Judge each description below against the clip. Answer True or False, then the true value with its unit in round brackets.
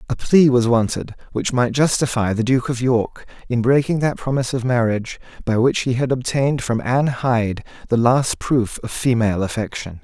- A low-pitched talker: True (125 Hz)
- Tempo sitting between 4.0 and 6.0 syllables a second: True (5.3 syllables/s)